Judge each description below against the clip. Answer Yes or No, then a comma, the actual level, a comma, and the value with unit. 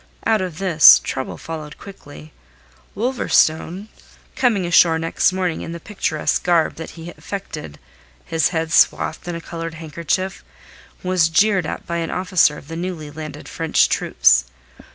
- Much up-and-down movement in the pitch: No, average, 2.8 semitones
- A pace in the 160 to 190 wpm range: No, average, 150 wpm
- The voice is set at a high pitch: No, medium, 170 Hz